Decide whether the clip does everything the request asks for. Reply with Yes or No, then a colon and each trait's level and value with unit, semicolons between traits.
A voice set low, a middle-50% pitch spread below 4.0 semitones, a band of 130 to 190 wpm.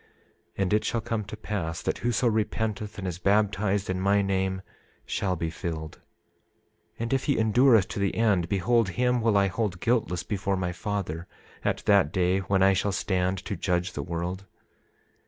Yes: low, 100 Hz; average, 2.9 semitones; average, 180 wpm